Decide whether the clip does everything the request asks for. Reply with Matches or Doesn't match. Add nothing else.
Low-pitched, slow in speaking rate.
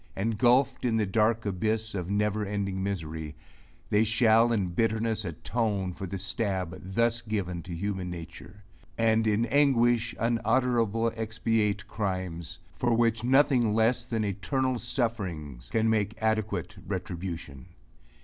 Matches